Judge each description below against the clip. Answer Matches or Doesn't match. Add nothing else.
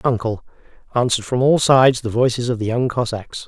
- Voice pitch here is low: Matches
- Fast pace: Doesn't match